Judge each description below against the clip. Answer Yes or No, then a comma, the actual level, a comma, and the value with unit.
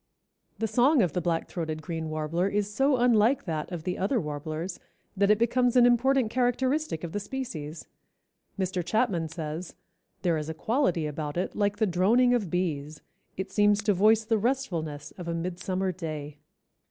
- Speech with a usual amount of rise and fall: No, wide, 5.9 semitones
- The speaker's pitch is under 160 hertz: No, medium, 185 Hz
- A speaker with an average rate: Yes, average, 175 wpm